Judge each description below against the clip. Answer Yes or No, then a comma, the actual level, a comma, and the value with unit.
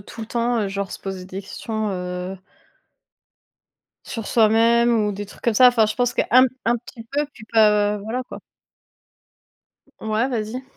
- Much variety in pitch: No, narrow, 2.6 semitones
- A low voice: No, high, 220 Hz